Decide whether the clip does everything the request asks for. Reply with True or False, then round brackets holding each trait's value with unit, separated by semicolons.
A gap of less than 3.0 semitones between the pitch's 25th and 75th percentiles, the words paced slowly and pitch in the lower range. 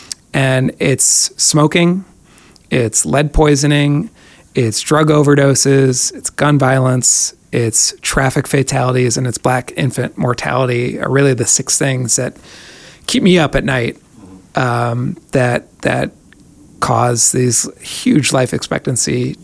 True (2.5 semitones; 120 wpm; 130 Hz)